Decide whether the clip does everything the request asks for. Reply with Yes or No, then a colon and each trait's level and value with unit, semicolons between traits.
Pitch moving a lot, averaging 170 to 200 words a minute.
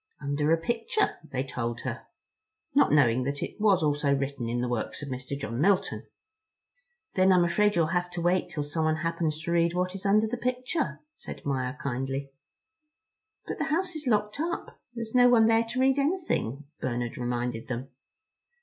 Yes: wide, 8.5 semitones; average, 180 wpm